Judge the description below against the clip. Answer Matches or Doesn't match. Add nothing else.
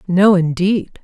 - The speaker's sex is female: Matches